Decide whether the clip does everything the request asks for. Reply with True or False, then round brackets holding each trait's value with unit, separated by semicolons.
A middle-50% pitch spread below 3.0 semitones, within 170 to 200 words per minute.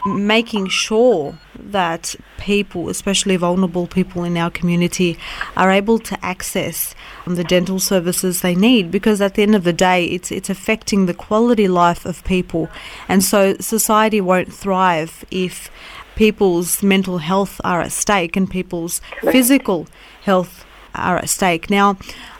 False (2.4 semitones; 145 wpm)